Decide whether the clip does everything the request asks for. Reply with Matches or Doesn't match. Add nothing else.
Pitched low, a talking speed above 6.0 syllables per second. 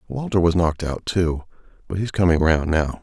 Doesn't match